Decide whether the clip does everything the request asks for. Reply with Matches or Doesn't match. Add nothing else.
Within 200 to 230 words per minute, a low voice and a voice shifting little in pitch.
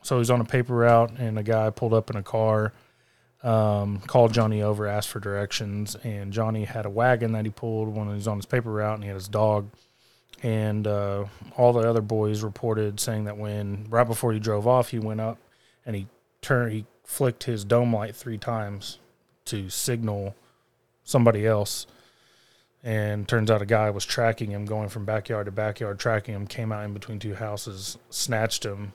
Matches